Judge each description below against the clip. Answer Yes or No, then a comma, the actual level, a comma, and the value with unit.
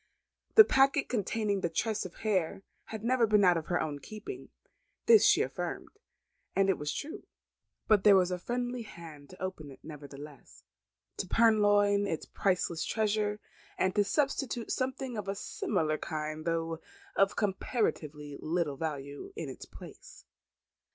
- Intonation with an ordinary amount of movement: No, wide, 5.7 semitones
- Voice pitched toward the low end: No, high, 195 Hz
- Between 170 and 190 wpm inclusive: No, average, 150 wpm